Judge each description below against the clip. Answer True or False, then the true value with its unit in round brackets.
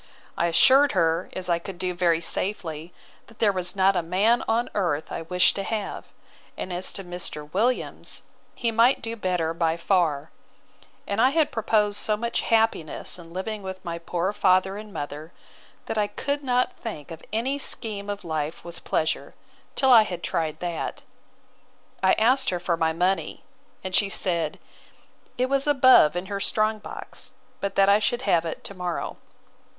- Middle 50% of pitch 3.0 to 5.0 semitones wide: True (4.5 semitones)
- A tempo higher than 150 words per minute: True (175 wpm)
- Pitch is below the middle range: False (190 Hz)